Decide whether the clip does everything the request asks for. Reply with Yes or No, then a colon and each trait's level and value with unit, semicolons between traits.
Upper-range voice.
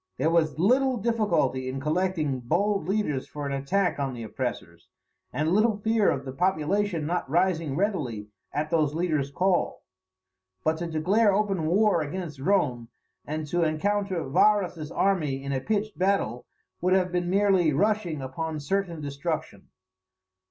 No: medium, 165 Hz